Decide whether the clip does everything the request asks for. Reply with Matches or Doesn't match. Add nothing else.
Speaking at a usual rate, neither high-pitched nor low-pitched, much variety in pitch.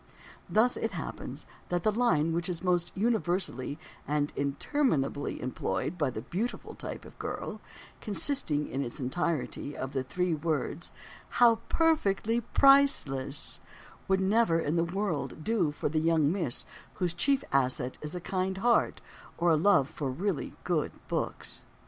Matches